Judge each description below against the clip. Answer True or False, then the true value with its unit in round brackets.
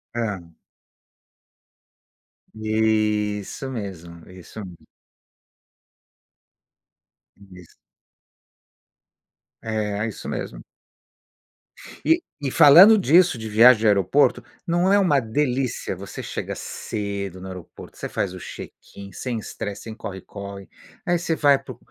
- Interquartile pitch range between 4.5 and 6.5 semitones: True (5.4 semitones)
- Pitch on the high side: False (110 Hz)